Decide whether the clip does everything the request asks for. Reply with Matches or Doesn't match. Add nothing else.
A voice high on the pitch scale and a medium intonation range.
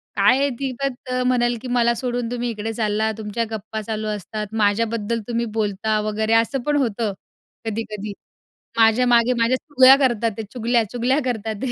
Doesn't match